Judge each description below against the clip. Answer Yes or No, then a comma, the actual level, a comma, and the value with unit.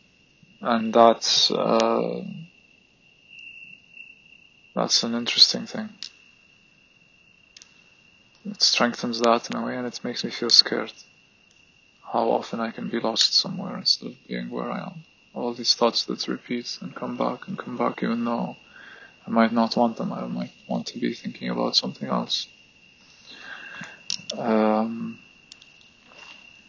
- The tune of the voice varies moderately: No, narrow, 2.2 semitones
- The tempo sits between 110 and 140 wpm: Yes, slow, 135 wpm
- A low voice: Yes, low, 115 Hz